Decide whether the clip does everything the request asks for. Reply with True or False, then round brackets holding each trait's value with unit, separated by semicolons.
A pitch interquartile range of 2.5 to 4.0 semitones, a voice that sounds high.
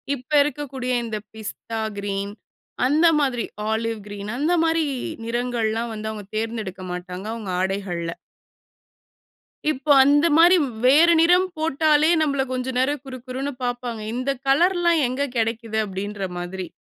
False (5.4 semitones; 245 Hz)